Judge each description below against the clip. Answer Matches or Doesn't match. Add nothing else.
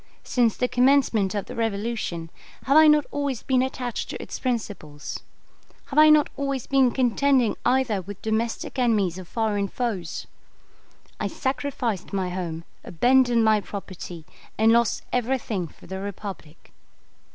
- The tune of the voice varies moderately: Matches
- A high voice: Matches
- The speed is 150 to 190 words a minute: Doesn't match